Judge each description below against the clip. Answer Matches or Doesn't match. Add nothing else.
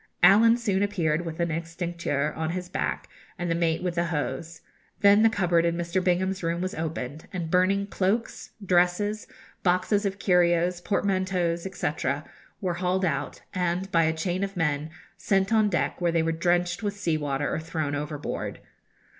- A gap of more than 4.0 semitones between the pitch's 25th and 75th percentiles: Doesn't match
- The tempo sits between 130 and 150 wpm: Doesn't match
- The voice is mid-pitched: Matches